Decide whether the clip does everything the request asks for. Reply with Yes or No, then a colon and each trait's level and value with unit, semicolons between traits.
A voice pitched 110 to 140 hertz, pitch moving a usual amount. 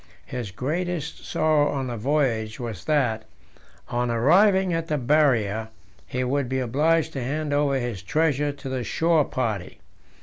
Yes: low, 135 Hz; average, 4.4 semitones